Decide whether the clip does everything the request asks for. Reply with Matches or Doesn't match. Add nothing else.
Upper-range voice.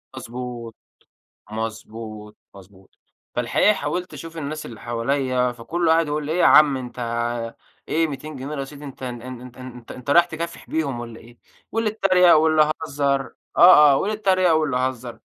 Doesn't match